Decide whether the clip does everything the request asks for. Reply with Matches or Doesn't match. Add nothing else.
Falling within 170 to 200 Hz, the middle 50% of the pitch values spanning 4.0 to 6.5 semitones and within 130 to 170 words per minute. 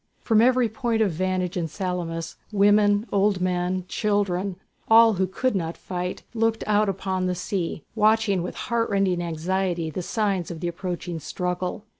Doesn't match